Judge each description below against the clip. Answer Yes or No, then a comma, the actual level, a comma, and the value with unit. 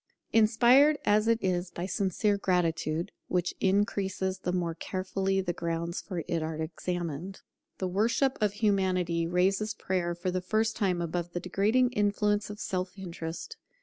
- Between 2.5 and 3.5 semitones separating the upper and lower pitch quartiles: Yes, average, 3.0 semitones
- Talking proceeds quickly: No, average, 150 wpm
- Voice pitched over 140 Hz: Yes, medium, 185 Hz